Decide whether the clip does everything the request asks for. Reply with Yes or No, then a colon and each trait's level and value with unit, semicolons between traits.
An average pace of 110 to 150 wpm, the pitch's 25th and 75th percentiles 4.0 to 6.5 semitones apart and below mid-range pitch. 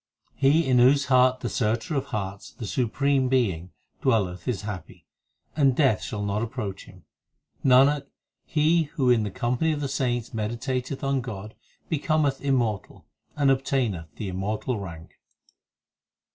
Yes: average, 145 wpm; average, 4.5 semitones; low, 125 Hz